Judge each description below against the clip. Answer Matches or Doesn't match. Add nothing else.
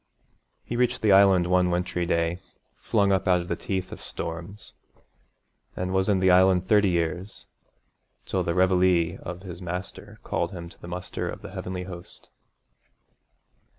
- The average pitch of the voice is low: Matches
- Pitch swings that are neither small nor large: Doesn't match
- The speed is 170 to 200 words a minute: Doesn't match